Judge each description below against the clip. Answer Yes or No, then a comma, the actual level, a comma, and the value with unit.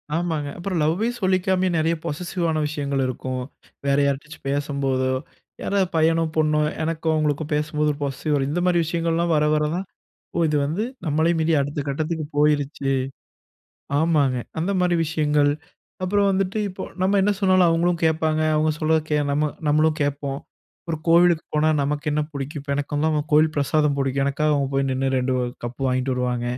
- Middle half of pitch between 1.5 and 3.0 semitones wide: Yes, average, 2.7 semitones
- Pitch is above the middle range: No, medium, 155 Hz